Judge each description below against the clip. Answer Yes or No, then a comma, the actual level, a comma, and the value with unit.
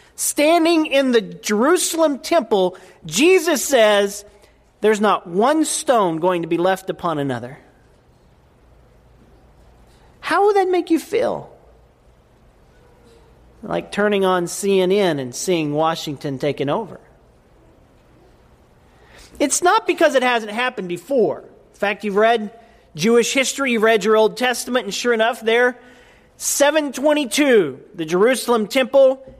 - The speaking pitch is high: Yes, high, 230 Hz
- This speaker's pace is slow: Yes, slow, 120 wpm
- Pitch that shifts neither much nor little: No, wide, 7.1 semitones